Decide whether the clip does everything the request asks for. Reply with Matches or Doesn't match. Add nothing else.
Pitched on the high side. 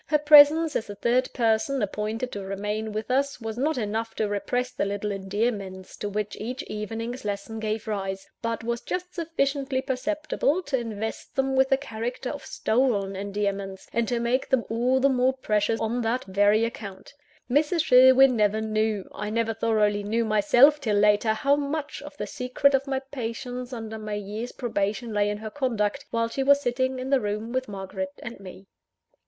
Matches